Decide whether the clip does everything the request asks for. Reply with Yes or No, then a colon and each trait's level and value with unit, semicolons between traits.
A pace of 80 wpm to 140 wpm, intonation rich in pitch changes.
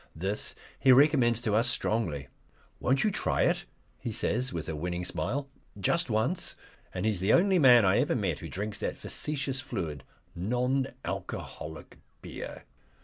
No: average, 160 wpm; wide, 6.2 semitones